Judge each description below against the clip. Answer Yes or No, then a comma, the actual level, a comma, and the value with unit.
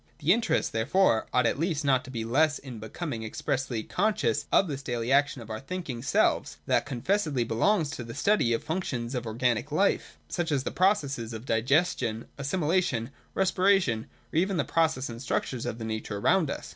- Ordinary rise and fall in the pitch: No, wide, 6.3 semitones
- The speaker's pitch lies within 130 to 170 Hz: Yes, low, 135 Hz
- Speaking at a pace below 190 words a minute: No, average, 195 wpm